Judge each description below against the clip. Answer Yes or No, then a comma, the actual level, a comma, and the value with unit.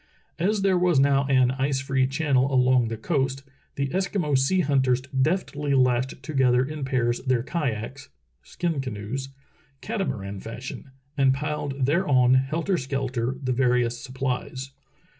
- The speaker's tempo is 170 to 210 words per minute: No, slow, 135 wpm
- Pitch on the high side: No, low, 135 Hz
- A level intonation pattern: Yes, narrow, 2.3 semitones